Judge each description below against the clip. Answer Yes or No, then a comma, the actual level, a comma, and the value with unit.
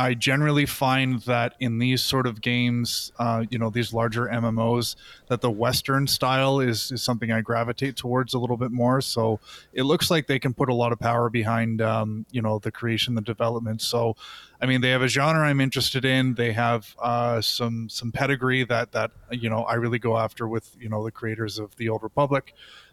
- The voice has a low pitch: Yes, low, 120 Hz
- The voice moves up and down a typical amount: No, narrow, 2.1 semitones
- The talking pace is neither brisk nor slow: No, fast, 210 wpm